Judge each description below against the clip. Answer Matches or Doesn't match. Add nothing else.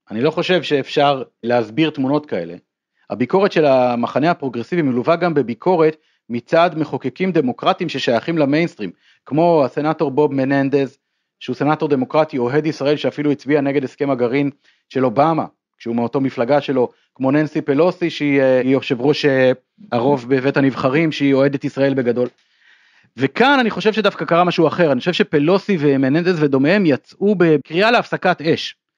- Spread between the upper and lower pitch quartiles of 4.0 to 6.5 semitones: Doesn't match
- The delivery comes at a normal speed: Matches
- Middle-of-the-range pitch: Matches